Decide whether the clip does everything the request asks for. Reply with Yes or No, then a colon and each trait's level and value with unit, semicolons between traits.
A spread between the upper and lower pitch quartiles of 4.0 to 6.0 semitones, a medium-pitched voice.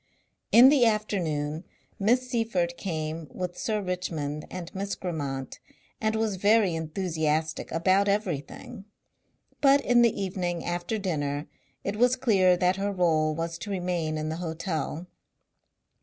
Yes: average, 4.3 semitones; medium, 180 Hz